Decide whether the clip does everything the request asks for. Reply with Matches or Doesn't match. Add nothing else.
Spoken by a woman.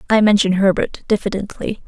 Matches